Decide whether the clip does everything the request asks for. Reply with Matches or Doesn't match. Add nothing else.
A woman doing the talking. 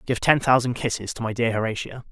Doesn't match